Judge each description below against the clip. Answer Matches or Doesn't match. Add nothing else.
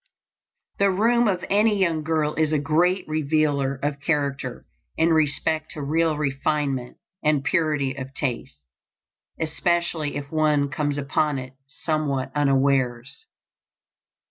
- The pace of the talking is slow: Matches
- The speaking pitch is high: Doesn't match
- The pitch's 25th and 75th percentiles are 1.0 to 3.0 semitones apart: Matches